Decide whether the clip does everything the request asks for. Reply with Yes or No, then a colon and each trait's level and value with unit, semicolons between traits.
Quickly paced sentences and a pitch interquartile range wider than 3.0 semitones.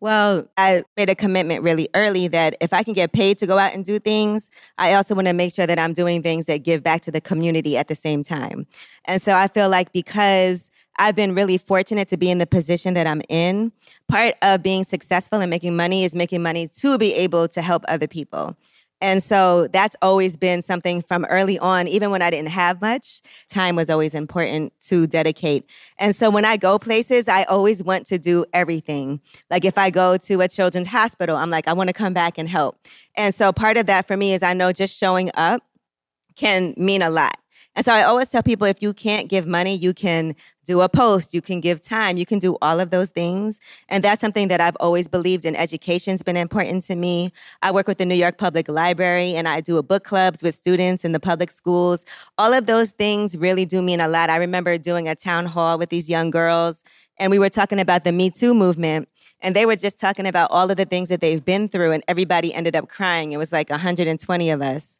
No: fast, 235 wpm; narrow, 2.5 semitones